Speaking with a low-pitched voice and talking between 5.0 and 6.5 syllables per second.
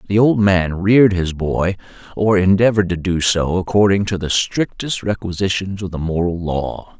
No: very low, 95 Hz; 4.8 syllables/s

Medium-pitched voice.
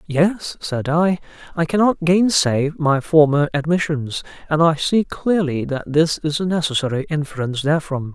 Yes: medium, 155 Hz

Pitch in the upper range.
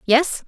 Yes: very high, 270 Hz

